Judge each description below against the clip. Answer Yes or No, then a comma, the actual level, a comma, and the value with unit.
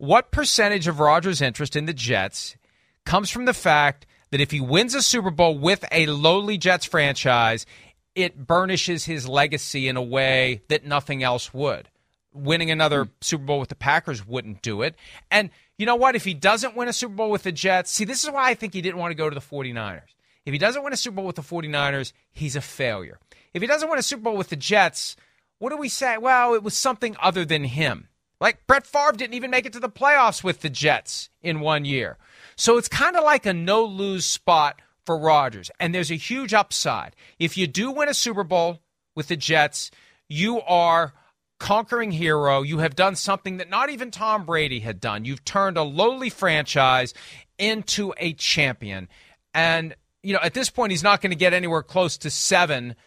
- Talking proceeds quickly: Yes, fast, 210 wpm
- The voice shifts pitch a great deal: Yes, wide, 6.7 semitones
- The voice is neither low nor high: Yes, medium, 175 Hz